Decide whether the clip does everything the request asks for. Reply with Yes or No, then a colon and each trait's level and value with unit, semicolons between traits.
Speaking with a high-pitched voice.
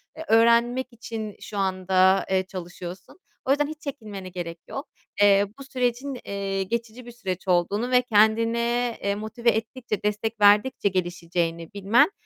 Yes: high, 210 Hz